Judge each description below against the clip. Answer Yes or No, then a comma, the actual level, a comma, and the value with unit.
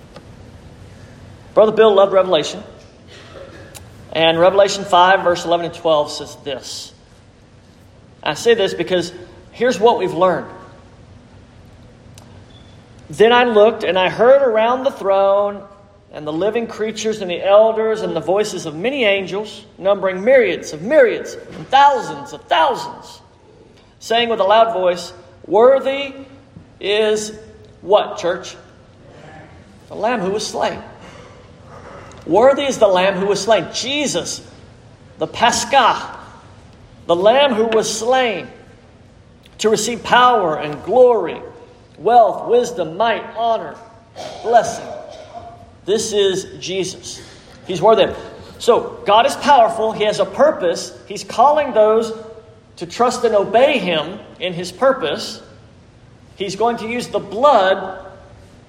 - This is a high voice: Yes, high, 200 Hz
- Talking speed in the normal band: No, slow, 125 wpm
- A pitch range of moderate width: No, wide, 6.5 semitones